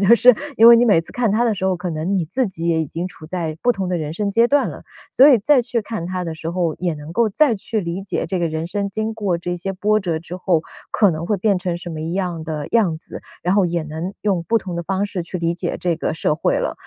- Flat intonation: No, average, 3.9 semitones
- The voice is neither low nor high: Yes, medium, 180 Hz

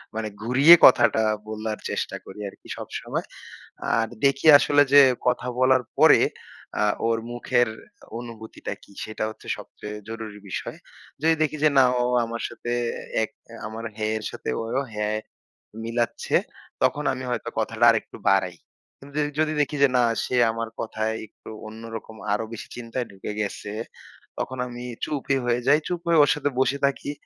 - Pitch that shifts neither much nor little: Yes, average, 3.7 semitones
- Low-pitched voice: Yes, low, 120 Hz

